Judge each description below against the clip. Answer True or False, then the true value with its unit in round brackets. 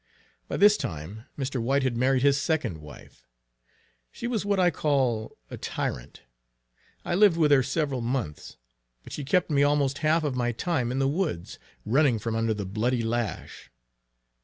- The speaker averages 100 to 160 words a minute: False (170 wpm)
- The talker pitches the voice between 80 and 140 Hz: True (135 Hz)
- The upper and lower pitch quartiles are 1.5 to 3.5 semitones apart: False (4.9 semitones)